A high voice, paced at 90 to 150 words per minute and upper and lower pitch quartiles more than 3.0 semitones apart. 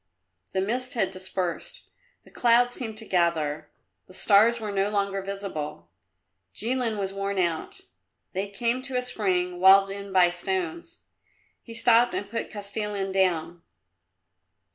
Yes: high, 200 Hz; average, 140 wpm; average, 3.7 semitones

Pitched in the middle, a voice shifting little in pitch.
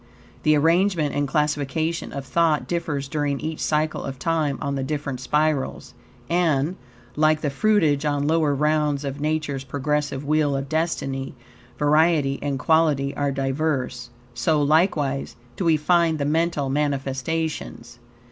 Yes: medium, 150 Hz; narrow, 2.3 semitones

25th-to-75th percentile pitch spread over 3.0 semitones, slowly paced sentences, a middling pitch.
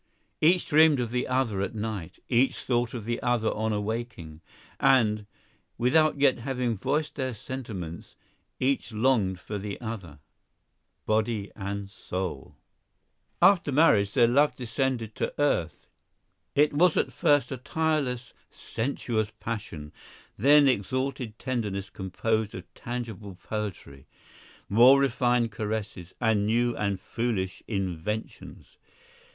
No: average, 4.4 semitones; slow, 125 wpm; low, 115 Hz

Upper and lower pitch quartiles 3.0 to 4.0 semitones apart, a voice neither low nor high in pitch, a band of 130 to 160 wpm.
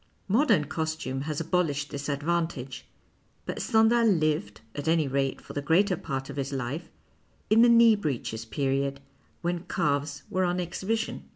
No: average, 4.5 semitones; medium, 155 Hz; average, 155 wpm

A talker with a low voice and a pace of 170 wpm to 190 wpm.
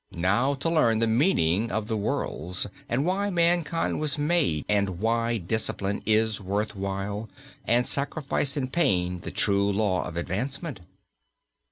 No: low, 110 Hz; average, 145 wpm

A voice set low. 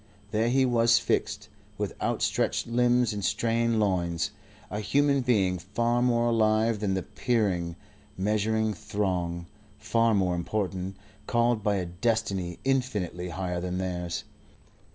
Yes: low, 105 Hz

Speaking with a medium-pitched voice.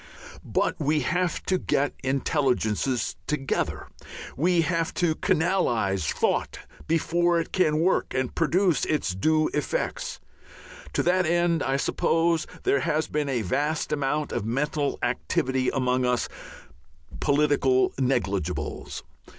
Yes: medium, 150 Hz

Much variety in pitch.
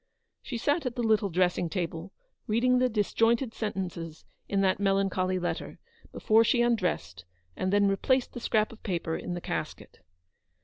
No: average, 4.3 semitones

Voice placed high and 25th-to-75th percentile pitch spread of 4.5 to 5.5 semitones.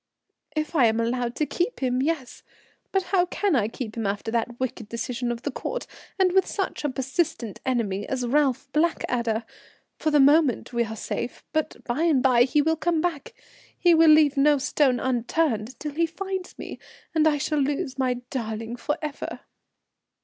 Yes: very high, 275 Hz; average, 4.8 semitones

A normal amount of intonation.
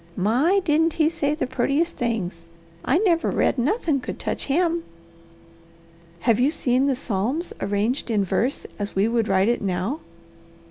No: wide, 6.9 semitones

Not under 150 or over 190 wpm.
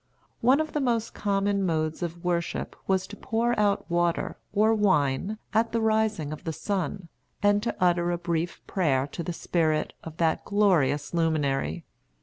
Yes: average, 165 wpm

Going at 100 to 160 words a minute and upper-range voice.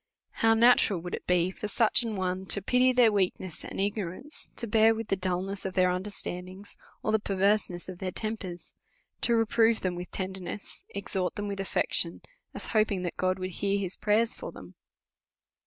No: average, 190 wpm; high, 195 Hz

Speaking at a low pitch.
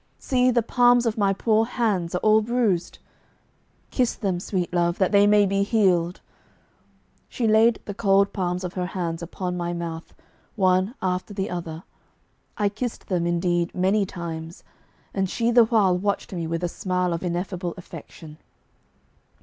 No: high, 190 Hz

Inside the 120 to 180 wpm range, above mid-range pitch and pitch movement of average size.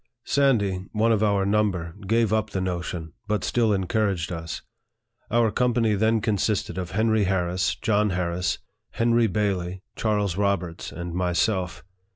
No: average, 140 wpm; low, 100 Hz; average, 3.4 semitones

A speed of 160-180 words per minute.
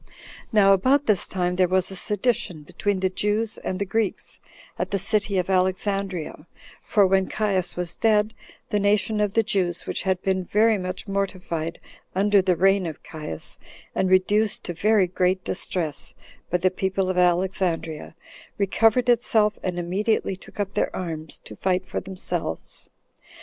Yes: average, 165 wpm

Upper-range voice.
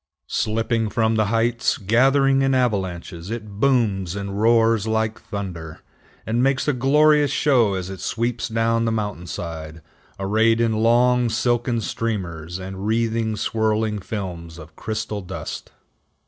No: low, 110 Hz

